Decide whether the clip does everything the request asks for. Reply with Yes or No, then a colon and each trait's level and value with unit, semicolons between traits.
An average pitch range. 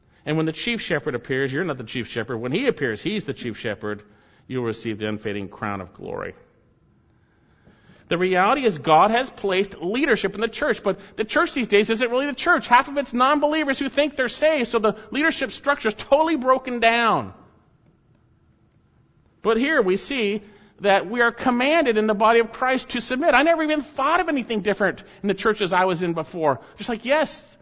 No: wide, 6.7 semitones